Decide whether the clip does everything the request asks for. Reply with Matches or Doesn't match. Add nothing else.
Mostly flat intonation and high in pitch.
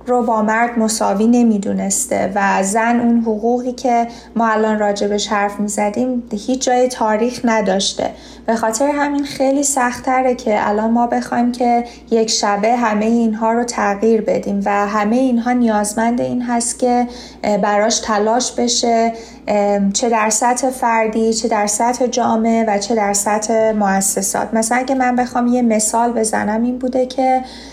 Matches